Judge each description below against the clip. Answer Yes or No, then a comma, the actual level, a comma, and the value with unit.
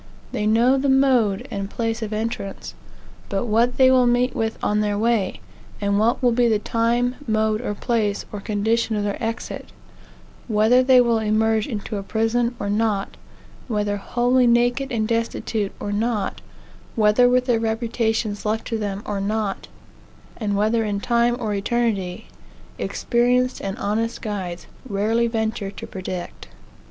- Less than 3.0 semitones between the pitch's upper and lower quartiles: Yes, narrow, 2.5 semitones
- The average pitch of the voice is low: No, high, 225 Hz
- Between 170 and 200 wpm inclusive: No, average, 155 wpm